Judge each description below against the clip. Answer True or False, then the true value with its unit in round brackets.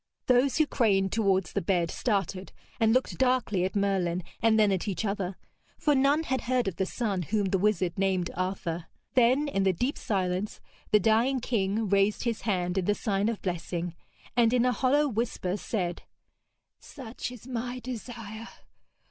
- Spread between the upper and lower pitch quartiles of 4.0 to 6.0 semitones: True (4.4 semitones)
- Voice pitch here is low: False (210 Hz)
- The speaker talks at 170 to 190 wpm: True (175 wpm)